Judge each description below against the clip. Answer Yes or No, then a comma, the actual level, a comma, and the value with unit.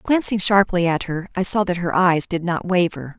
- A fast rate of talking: Yes, fast, 225 wpm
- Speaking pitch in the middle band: Yes, medium, 180 Hz